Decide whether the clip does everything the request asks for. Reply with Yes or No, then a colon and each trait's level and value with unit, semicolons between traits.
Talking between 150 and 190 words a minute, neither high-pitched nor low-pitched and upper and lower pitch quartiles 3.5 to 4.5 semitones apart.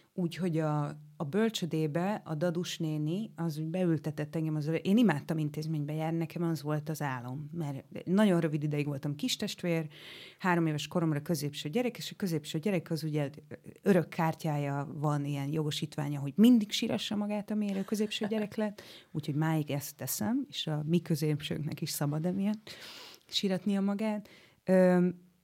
Yes: fast, 155 wpm; medium, 165 Hz; average, 4.1 semitones